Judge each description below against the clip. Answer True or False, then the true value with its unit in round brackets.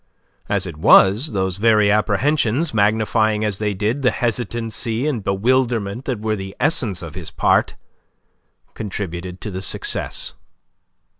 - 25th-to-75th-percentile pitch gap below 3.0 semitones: False (3.3 semitones)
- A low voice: True (105 Hz)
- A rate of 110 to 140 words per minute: True (135 wpm)